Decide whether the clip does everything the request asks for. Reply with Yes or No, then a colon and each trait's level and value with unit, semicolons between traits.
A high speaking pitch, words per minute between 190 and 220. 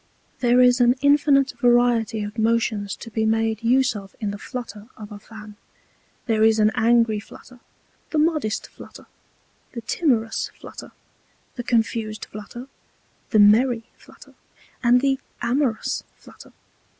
No: high, 230 Hz; average, 140 wpm